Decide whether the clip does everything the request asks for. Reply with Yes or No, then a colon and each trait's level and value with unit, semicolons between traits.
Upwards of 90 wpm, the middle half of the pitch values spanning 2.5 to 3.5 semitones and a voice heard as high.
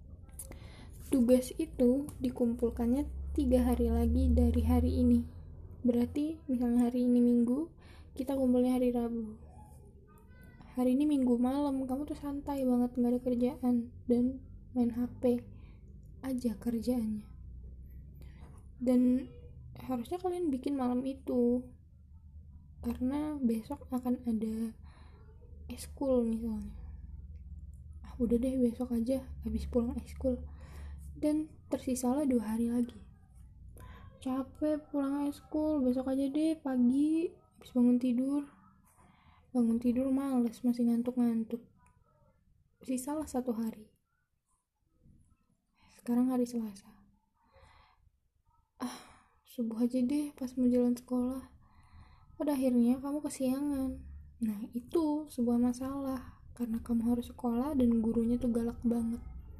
Yes: average, 110 wpm; average, 2.8 semitones; high, 245 Hz